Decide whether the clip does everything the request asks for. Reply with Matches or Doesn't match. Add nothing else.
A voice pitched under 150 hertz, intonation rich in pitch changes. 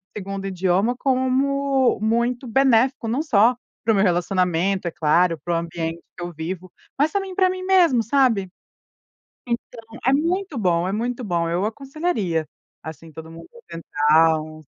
Doesn't match